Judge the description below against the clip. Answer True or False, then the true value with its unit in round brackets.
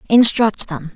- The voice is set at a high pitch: True (210 Hz)